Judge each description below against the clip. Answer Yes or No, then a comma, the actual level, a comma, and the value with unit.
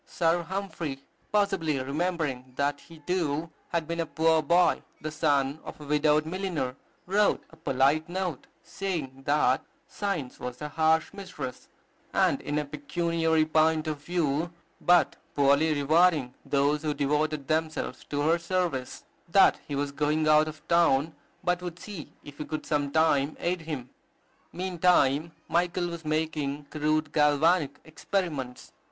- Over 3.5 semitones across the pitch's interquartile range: No, average, 2.8 semitones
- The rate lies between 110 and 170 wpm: Yes, average, 145 wpm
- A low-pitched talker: No, medium, 155 Hz